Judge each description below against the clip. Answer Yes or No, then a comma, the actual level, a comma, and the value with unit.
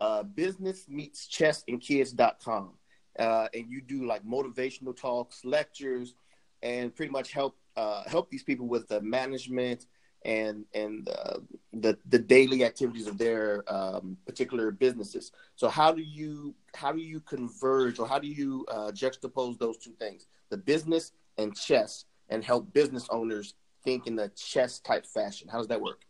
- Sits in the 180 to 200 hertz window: No, low, 130 Hz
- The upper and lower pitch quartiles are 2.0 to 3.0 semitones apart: No, average, 4.2 semitones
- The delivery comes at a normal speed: Yes, average, 165 wpm